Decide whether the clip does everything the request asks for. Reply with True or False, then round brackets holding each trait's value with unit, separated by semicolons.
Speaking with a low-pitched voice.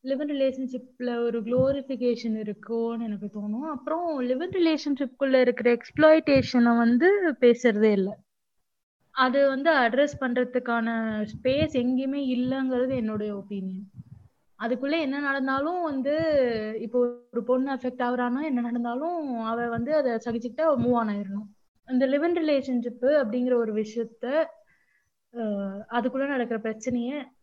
False (250 Hz)